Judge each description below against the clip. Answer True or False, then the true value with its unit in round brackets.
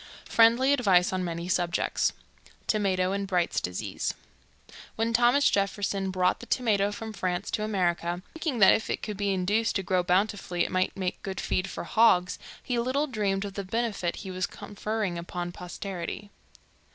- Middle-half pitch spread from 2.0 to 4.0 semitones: True (3.3 semitones)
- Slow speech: False (165 wpm)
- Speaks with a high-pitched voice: True (195 Hz)